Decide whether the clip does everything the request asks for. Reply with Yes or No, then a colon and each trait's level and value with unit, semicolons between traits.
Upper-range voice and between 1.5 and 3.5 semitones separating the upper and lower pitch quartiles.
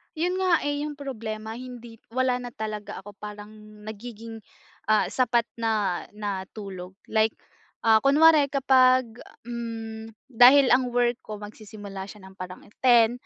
Yes: high, 225 Hz; average, 3.2 semitones